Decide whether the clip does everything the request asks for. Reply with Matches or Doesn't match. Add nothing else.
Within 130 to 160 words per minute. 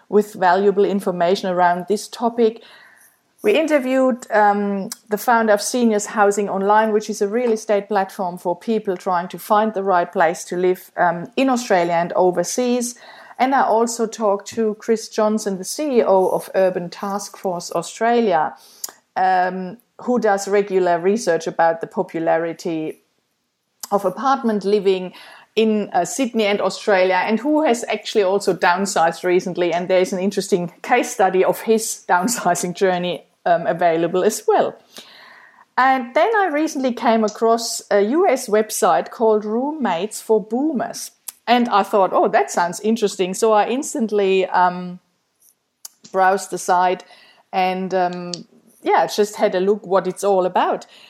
Matches